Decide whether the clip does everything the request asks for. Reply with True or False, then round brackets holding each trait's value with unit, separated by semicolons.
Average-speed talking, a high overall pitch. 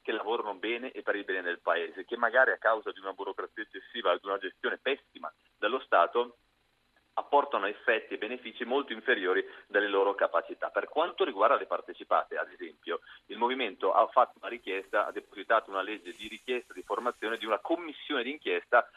False (180 wpm; 390 Hz)